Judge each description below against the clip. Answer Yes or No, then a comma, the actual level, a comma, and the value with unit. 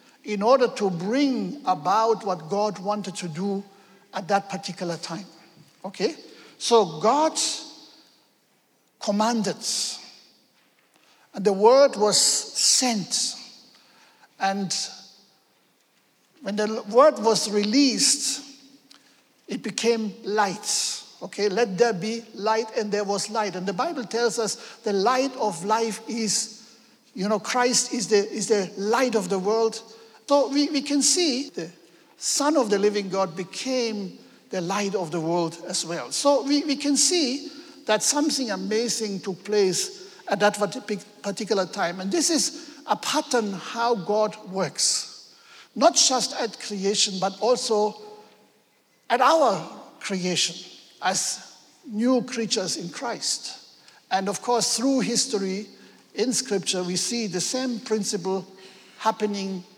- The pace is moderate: No, slow, 130 wpm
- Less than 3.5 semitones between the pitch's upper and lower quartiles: No, average, 3.9 semitones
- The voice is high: Yes, high, 215 Hz